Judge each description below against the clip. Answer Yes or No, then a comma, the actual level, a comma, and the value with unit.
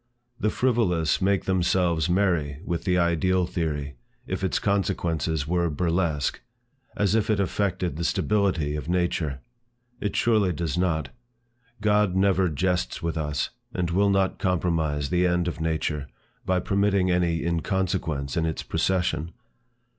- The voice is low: Yes, very low, 90 Hz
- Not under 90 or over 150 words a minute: Yes, average, 140 wpm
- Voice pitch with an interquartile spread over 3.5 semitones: No, average, 3.0 semitones